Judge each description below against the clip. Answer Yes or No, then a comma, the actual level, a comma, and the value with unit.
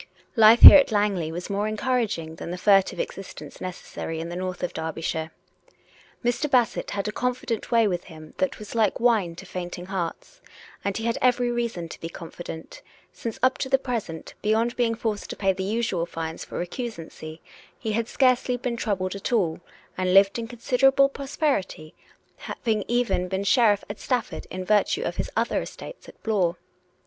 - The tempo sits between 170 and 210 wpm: Yes, average, 185 wpm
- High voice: Yes, high, 210 Hz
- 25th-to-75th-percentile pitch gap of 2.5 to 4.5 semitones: No, average, 5.1 semitones